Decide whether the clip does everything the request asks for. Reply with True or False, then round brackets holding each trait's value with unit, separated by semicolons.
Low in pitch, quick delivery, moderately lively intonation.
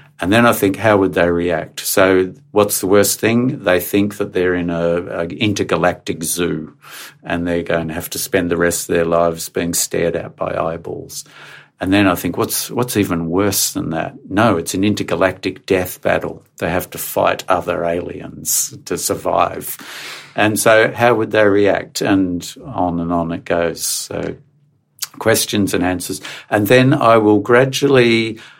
False (95 Hz; 175 wpm; 4.3 semitones)